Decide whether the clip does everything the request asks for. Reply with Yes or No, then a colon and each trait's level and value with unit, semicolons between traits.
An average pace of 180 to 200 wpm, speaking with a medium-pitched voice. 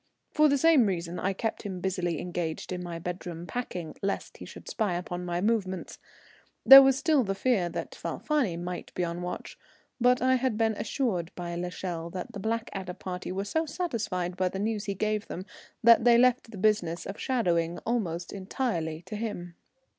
No: average, 190 wpm; high, 195 Hz